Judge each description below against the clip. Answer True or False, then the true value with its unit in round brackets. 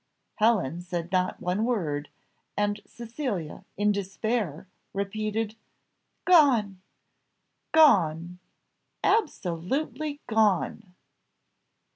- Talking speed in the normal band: False (70 wpm)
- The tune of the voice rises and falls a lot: False (4.6 semitones)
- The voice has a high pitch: True (205 Hz)